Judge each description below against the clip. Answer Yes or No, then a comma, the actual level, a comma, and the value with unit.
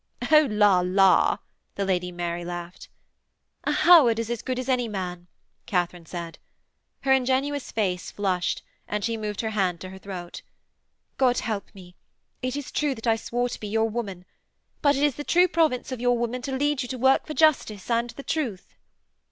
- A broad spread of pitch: Yes, wide, 5.8 semitones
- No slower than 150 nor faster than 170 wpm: No, average, 190 wpm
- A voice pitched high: Yes, high, 225 Hz